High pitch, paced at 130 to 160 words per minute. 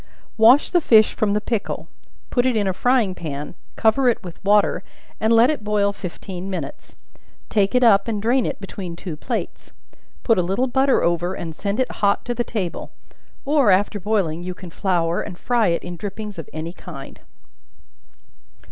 No: high, 205 Hz; average, 185 wpm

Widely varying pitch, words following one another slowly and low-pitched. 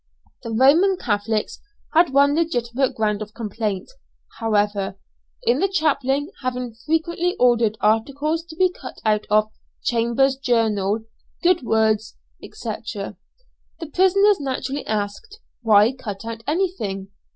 No: wide, 6.6 semitones; slow, 120 wpm; high, 245 Hz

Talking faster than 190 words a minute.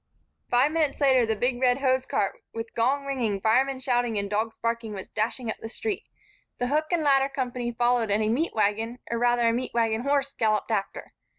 Yes: average, 200 wpm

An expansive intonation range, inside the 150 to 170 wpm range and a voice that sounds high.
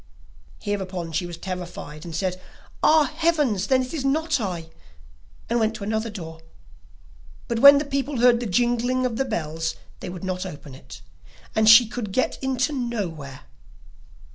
Yes: wide, 6.6 semitones; average, 165 wpm; high, 215 Hz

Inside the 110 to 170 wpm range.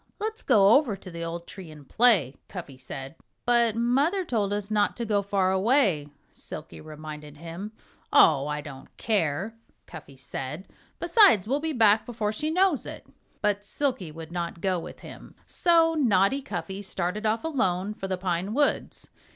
Yes: average, 165 wpm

